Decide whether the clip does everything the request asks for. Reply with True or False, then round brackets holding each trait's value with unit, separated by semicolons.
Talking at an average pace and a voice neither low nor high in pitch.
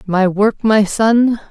False (160 wpm; 210 Hz)